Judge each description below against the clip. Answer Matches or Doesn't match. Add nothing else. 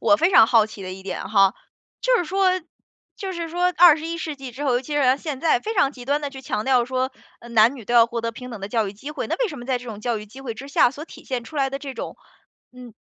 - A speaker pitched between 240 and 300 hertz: Matches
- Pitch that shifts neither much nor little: Matches